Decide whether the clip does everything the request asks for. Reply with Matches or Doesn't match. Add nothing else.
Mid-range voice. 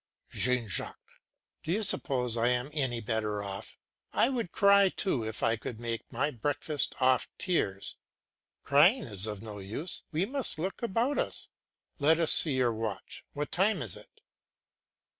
Doesn't match